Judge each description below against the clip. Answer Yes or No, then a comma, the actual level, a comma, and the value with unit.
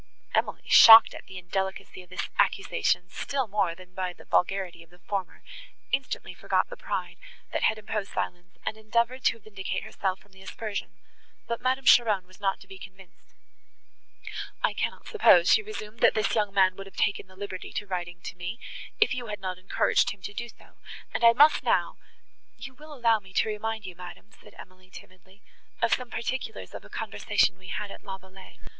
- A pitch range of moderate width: Yes, average, 3.4 semitones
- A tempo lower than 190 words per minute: No, average, 195 wpm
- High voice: Yes, high, 200 Hz